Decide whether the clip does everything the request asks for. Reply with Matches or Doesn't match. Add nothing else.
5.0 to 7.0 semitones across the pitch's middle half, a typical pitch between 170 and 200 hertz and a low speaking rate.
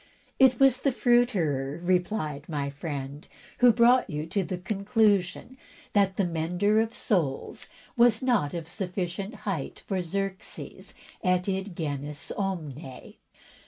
Matches